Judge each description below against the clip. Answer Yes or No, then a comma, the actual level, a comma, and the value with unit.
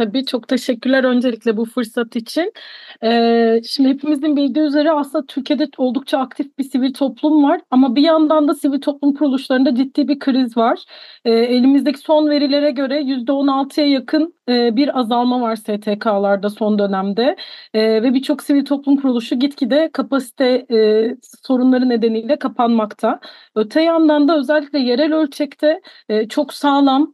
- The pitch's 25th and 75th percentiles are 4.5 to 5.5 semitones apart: No, average, 3.7 semitones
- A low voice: No, very high, 270 Hz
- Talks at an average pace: No, fast, 145 wpm